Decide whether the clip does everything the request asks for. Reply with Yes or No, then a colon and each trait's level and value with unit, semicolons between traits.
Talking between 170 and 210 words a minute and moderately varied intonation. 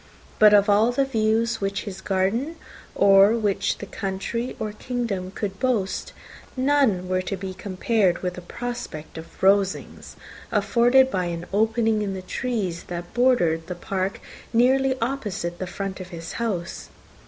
No: average, 155 wpm; average, 4.0 semitones